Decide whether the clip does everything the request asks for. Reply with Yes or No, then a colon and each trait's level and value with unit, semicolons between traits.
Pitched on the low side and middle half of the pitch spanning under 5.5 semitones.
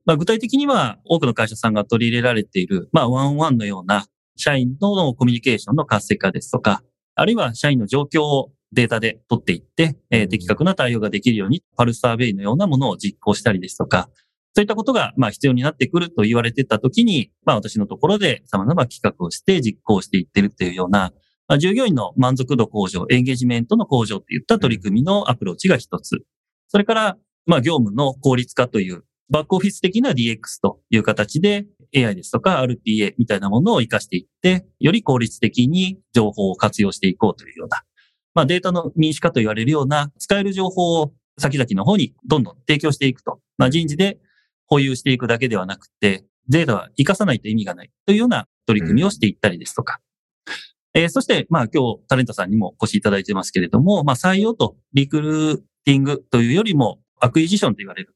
No: low, 130 Hz; wide, 6.8 semitones